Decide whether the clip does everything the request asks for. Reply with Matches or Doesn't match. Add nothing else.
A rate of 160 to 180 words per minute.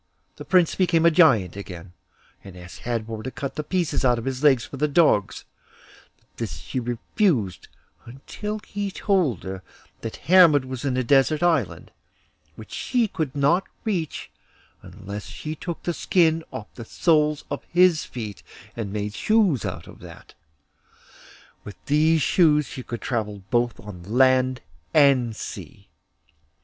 Doesn't match